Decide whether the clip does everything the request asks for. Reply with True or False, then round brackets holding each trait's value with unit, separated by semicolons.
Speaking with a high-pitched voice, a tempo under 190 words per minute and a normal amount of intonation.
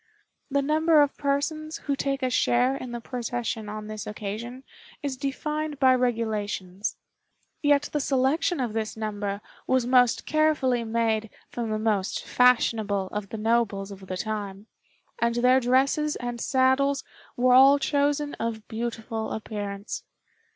True (240 Hz; 145 wpm; 4.2 semitones)